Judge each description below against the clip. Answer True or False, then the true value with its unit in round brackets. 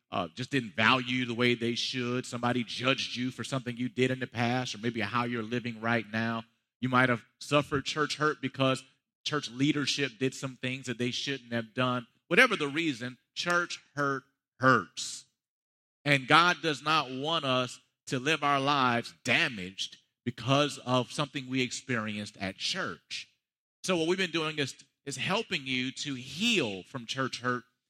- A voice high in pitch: False (130 Hz)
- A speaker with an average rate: True (170 wpm)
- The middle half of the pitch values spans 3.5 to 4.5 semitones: False (2.7 semitones)